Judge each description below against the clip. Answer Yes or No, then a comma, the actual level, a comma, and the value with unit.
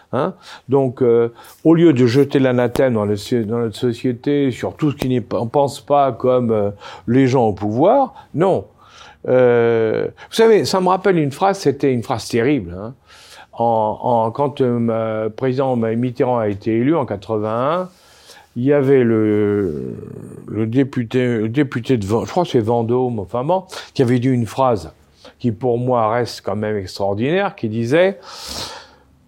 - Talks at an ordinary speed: Yes, average, 170 wpm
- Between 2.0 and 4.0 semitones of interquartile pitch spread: Yes, average, 3.5 semitones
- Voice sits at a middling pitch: No, low, 125 Hz